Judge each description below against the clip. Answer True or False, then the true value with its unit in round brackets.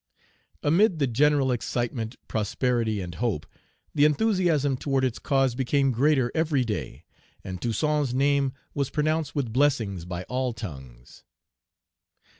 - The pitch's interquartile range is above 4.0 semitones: True (4.6 semitones)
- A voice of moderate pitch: False (130 Hz)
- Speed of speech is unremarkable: False (125 wpm)